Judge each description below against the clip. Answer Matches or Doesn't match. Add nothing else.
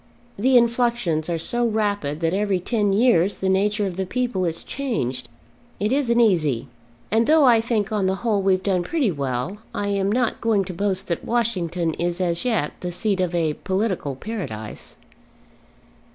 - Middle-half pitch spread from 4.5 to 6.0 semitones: Matches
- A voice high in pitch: Matches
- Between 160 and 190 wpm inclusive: Matches